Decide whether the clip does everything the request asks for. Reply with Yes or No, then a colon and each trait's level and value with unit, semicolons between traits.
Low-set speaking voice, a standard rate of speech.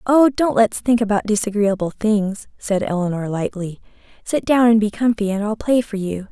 No: high, 215 Hz; average, 190 wpm